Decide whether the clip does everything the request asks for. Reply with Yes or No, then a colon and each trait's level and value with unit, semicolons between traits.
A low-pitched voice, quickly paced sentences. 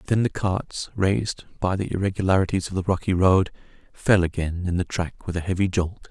No: very low, 95 Hz; average, 195 wpm